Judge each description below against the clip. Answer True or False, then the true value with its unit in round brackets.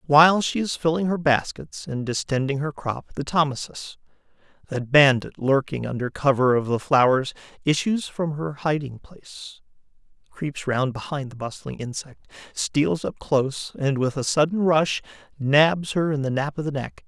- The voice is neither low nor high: True (145 Hz)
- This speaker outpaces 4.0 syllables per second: True (4.7 syllables/s)